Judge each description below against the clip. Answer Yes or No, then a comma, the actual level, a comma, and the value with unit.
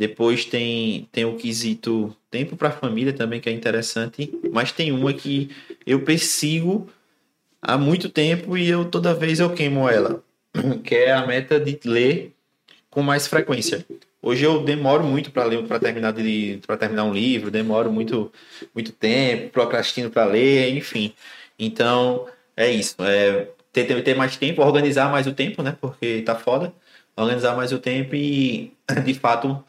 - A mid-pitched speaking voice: No, low, 130 Hz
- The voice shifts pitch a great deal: No, average, 4.1 semitones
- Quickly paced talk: No, average, 160 wpm